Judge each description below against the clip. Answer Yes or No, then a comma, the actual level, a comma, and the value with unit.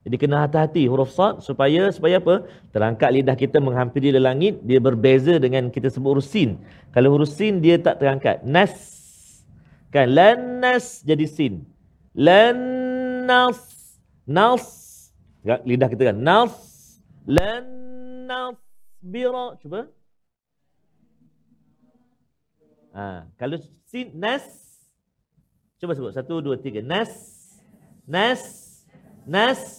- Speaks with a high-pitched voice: No, medium, 170 Hz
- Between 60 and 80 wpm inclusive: No, average, 110 wpm